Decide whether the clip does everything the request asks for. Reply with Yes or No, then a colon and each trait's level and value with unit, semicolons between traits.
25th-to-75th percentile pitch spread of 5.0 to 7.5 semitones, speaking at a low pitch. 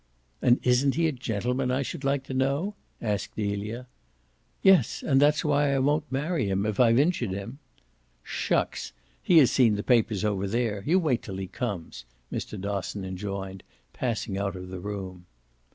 Yes: wide, 5.6 semitones; low, 115 Hz